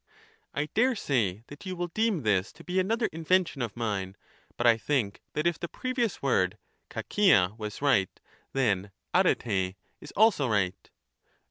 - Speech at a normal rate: Yes, average, 150 wpm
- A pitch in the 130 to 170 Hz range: Yes, low, 135 Hz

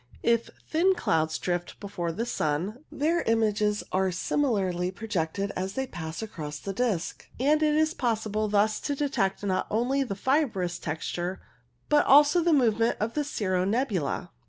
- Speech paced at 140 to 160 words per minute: Yes, average, 155 wpm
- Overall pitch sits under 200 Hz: No, high, 215 Hz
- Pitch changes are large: Yes, wide, 6.4 semitones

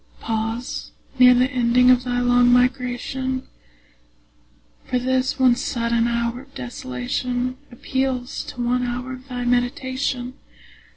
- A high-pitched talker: Yes, very high, 250 Hz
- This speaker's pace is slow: Yes, slow, 120 wpm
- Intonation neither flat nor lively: No, narrow, 1.0 semitones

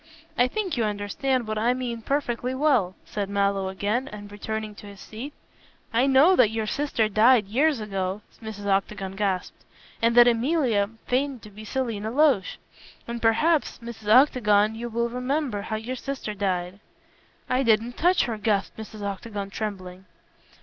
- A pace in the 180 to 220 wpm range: No, average, 160 wpm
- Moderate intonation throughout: Yes, average, 3.7 semitones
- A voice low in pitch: No, high, 220 Hz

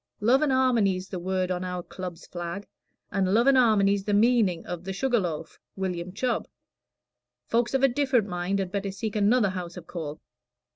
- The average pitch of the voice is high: Yes, high, 195 Hz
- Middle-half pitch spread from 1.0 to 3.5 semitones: No, average, 4.4 semitones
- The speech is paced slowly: No, average, 185 wpm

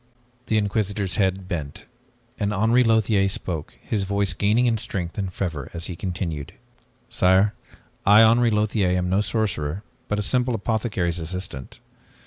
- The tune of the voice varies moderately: Yes, average, 3.2 semitones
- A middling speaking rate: Yes, average, 145 wpm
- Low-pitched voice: Yes, low, 100 Hz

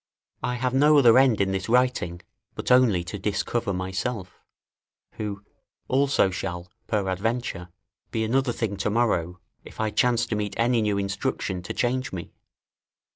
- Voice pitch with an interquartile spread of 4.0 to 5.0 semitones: Yes, average, 4.6 semitones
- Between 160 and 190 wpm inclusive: No, average, 150 wpm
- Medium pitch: No, low, 110 Hz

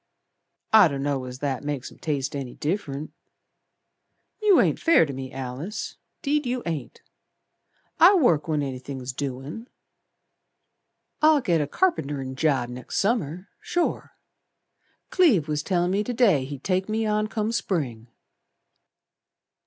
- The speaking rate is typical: No, slow, 130 wpm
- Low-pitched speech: No, medium, 155 Hz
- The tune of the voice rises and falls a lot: Yes, wide, 8.0 semitones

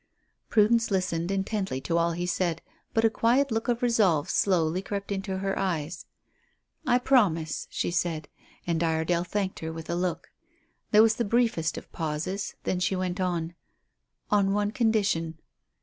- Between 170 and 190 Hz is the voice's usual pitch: Yes, medium, 185 Hz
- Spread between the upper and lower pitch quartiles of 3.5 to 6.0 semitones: Yes, average, 4.0 semitones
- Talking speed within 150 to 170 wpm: Yes, average, 160 wpm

